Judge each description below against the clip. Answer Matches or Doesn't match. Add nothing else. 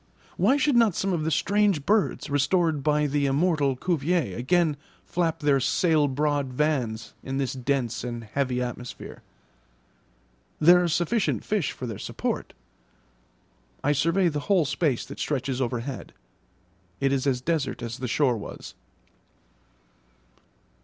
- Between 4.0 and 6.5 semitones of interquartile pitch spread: Matches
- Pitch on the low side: Doesn't match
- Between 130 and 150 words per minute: Matches